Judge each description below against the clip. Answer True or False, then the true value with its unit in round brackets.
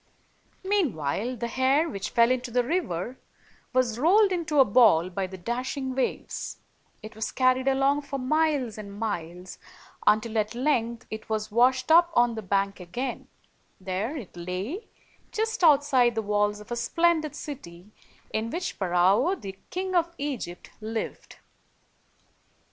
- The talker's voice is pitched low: False (240 Hz)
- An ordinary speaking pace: True (150 wpm)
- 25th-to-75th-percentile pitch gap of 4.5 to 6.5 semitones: True (5.5 semitones)